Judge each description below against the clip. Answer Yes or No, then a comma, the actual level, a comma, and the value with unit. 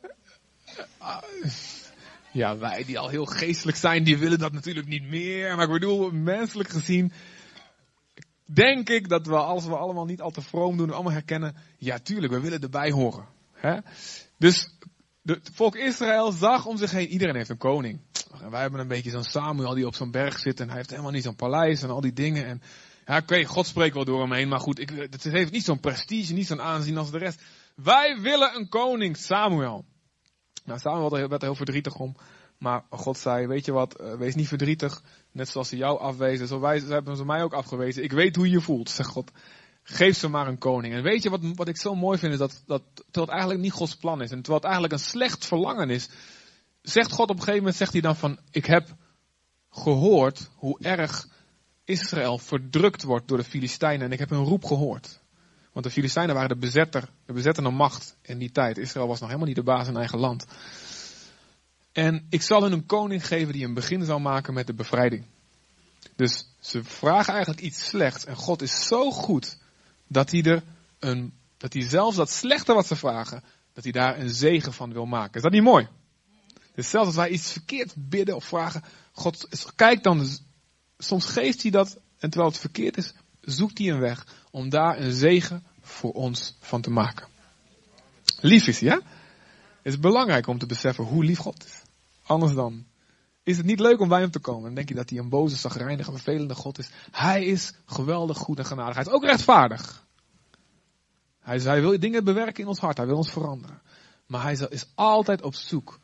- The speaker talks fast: Yes, fast, 205 wpm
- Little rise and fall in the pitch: No, wide, 5.4 semitones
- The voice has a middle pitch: Yes, medium, 150 Hz